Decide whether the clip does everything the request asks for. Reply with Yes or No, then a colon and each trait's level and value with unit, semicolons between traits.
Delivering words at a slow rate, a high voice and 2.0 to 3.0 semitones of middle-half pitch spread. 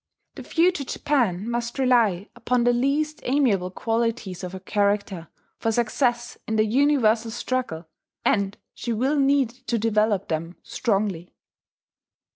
No: slow, 130 wpm; high, 230 Hz; average, 4.1 semitones